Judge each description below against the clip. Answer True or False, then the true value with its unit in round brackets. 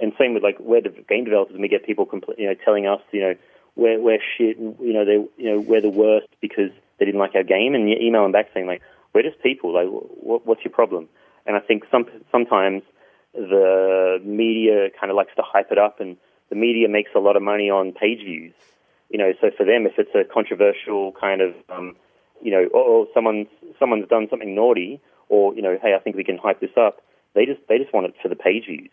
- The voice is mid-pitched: False (110 Hz)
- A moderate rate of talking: False (245 wpm)